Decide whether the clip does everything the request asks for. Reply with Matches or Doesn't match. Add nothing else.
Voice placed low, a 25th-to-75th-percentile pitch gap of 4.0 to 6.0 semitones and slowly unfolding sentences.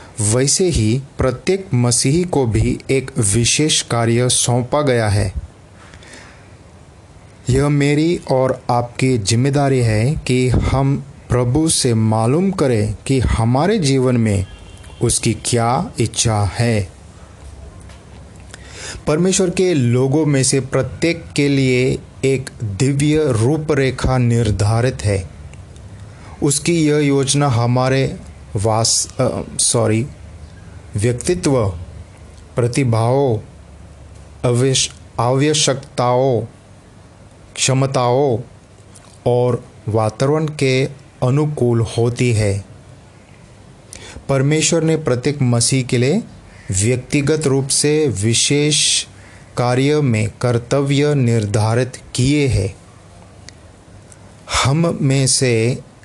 Matches